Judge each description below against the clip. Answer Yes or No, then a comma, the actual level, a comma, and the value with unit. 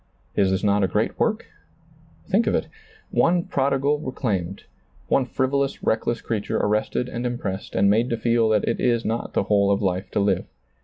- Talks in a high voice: No, low, 115 Hz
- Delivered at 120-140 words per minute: No, average, 190 wpm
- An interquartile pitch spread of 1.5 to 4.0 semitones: No, average, 4.4 semitones